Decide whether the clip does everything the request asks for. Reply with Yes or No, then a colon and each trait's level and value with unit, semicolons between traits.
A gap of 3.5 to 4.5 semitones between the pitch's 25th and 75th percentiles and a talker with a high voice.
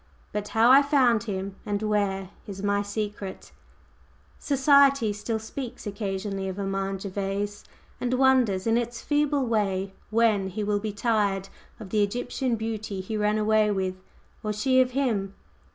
No: average, 3.1 semitones; high, 210 Hz